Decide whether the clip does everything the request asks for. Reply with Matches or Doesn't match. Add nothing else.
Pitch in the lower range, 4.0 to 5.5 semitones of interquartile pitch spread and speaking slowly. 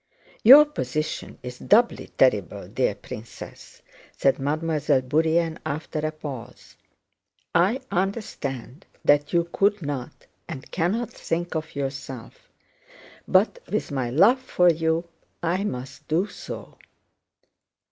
Doesn't match